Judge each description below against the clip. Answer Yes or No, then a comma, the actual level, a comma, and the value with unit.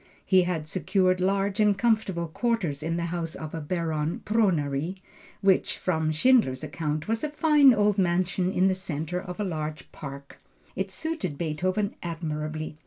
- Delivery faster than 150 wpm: Yes, average, 160 wpm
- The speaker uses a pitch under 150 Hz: No, medium, 180 Hz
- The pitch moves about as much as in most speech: Yes, average, 4.1 semitones